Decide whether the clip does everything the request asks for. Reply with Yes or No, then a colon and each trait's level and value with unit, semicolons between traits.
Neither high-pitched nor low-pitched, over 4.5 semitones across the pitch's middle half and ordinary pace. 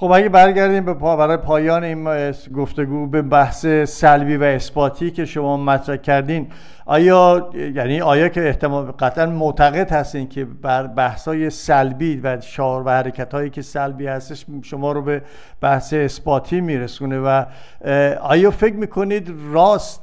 No: medium, 145 Hz; average, 3.0 semitones; average, 145 wpm